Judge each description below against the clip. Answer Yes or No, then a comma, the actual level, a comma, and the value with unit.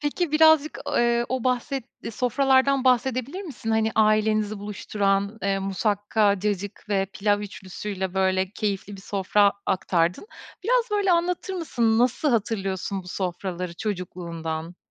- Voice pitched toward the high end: Yes, high, 210 Hz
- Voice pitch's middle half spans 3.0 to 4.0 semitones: No, average, 4.9 semitones